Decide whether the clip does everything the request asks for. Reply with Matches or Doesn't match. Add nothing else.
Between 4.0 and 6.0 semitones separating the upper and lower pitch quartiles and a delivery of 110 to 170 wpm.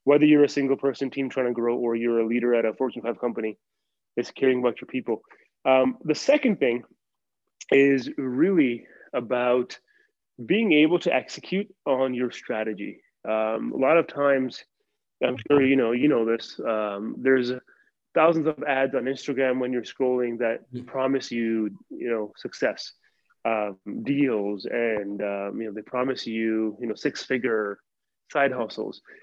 Doesn't match